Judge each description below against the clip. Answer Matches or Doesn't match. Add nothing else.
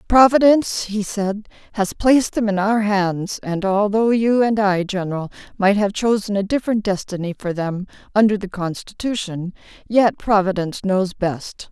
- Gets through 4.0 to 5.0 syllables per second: Matches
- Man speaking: Doesn't match